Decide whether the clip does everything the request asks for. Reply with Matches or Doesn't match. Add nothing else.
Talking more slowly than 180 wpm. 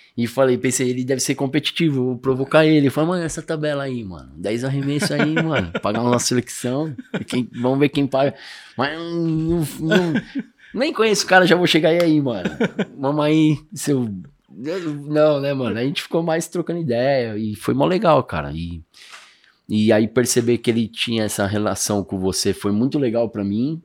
Doesn't match